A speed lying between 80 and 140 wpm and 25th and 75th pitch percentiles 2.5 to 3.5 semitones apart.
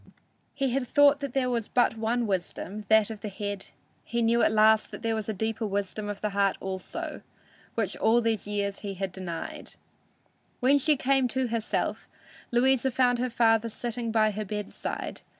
No: average, 180 wpm; average, 3.0 semitones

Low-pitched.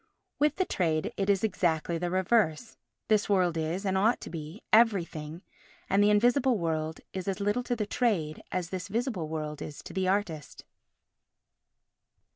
No: high, 190 Hz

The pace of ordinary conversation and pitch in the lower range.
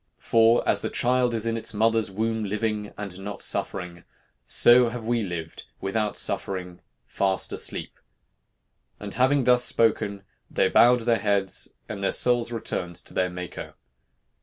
Yes: average, 150 wpm; low, 110 Hz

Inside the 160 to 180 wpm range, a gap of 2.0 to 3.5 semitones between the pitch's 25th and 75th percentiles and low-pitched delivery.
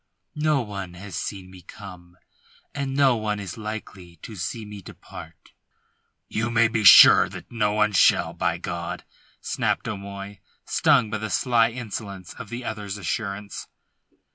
No: average, 150 wpm; narrow, 2.6 semitones; low, 105 Hz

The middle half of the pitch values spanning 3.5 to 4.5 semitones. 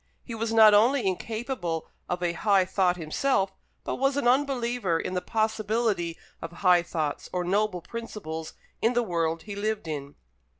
No: average, 4.9 semitones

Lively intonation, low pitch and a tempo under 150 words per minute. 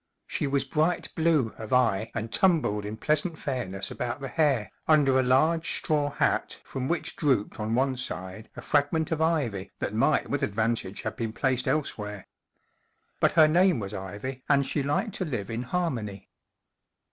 No: wide, 5.8 semitones; low, 130 Hz; average, 180 wpm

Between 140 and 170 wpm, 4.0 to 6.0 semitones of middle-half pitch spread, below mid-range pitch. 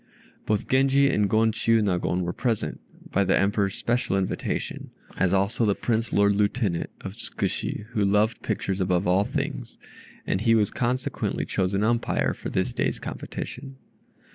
No: average, 150 wpm; average, 2.9 semitones; low, 105 Hz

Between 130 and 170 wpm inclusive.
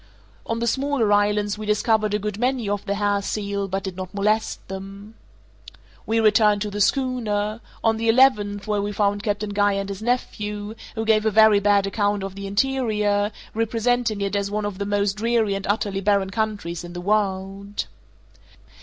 No: average, 185 wpm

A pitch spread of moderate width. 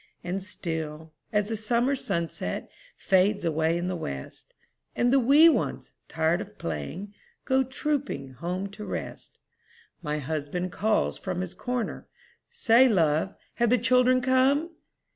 No: wide, 7.2 semitones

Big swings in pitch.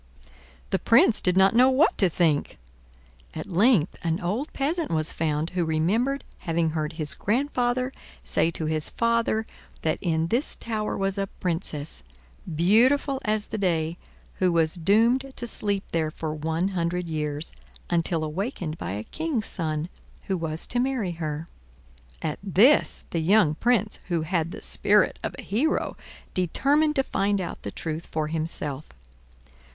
Yes: wide, 6.2 semitones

